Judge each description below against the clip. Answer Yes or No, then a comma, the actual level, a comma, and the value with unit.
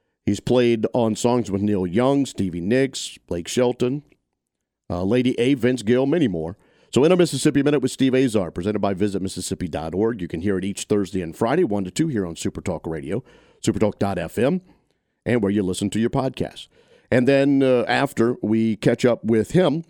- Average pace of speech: Yes, average, 185 wpm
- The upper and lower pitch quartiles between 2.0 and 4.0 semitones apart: No, average, 4.9 semitones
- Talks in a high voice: No, low, 110 Hz